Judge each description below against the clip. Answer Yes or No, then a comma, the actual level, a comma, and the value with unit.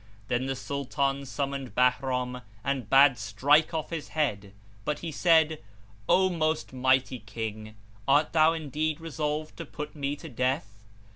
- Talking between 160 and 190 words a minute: No, average, 145 wpm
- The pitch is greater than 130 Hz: Yes, medium, 140 Hz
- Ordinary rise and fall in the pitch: Yes, average, 3.6 semitones